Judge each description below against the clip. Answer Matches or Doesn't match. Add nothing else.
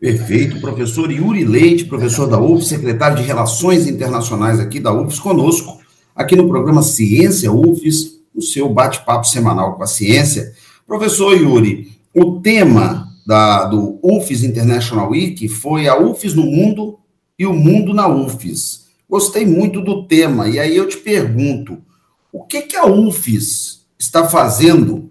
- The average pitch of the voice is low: Doesn't match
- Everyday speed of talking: Matches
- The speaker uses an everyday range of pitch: Doesn't match